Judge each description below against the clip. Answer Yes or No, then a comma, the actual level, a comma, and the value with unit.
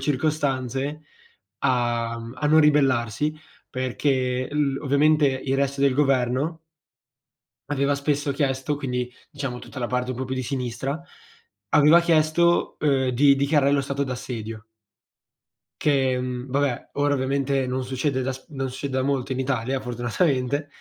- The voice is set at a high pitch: No, low, 135 Hz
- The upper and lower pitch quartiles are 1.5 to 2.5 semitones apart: Yes, narrow, 2.0 semitones